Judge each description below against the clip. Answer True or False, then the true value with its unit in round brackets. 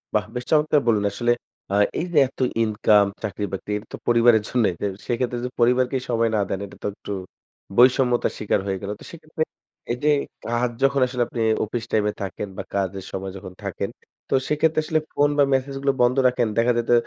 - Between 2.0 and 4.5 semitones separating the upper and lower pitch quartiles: True (3.7 semitones)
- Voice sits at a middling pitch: False (120 Hz)